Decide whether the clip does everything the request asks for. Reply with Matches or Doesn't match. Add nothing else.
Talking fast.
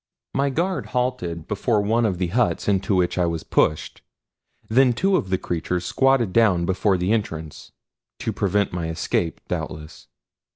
Doesn't match